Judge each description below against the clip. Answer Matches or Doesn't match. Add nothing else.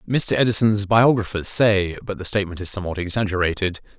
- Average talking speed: Matches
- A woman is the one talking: Doesn't match